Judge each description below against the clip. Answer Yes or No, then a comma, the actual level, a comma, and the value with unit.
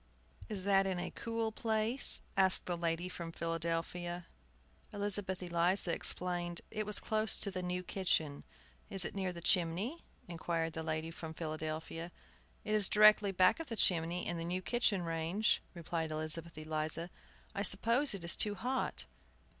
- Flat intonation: No, average, 3.5 semitones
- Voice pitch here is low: No, medium, 180 Hz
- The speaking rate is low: No, average, 160 wpm